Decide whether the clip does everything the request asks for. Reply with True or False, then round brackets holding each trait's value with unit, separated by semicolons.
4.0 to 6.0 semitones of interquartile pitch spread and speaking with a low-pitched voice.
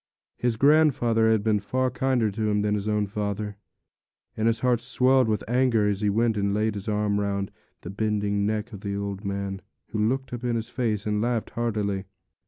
False (2.5 semitones; 105 Hz)